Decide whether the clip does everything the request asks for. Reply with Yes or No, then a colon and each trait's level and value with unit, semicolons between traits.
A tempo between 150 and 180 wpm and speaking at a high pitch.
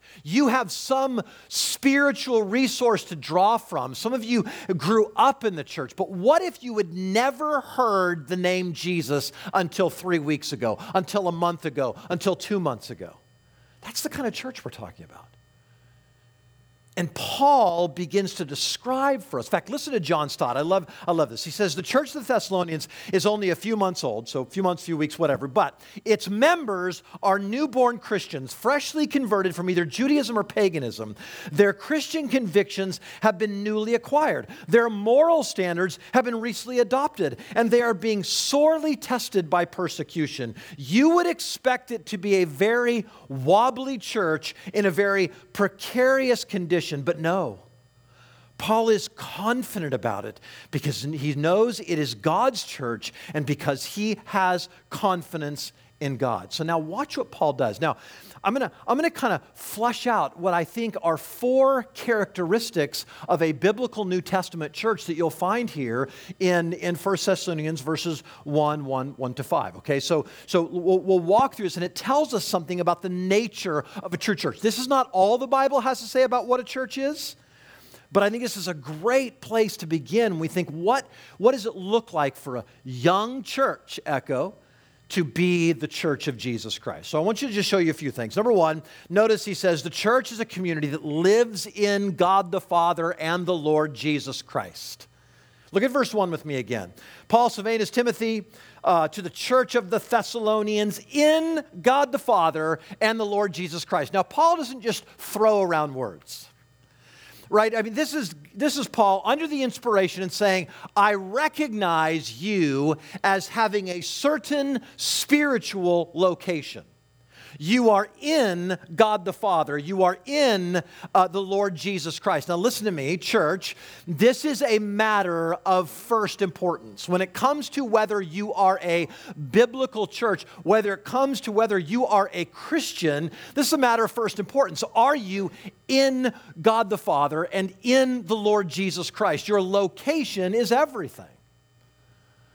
Yes: average, 175 wpm; high, 195 Hz